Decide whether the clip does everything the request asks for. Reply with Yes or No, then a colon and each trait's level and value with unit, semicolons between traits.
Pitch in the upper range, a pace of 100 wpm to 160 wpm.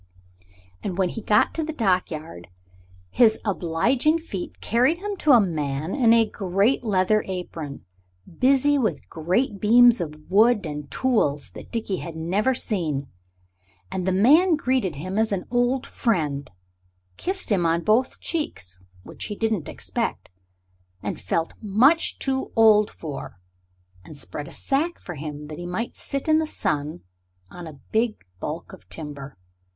Yes: high, 200 Hz; average, 155 wpm